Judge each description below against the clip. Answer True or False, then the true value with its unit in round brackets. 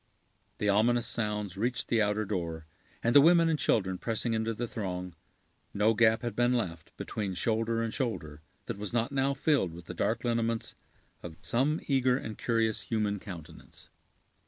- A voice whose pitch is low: True (110 Hz)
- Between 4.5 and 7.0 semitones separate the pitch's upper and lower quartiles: False (3.4 semitones)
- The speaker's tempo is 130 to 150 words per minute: False (170 wpm)